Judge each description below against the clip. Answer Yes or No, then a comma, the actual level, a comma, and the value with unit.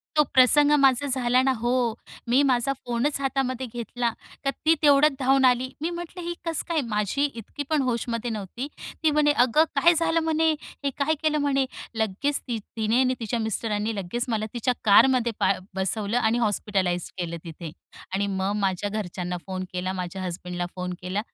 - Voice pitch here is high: Yes, high, 240 Hz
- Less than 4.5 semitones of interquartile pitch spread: No, wide, 5.4 semitones